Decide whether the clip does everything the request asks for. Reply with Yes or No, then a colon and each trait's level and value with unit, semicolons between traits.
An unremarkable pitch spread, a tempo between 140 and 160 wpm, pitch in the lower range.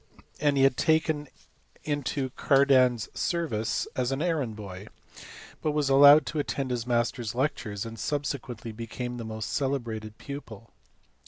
Yes: average, 4.0 semitones; average, 155 wpm; low, 130 Hz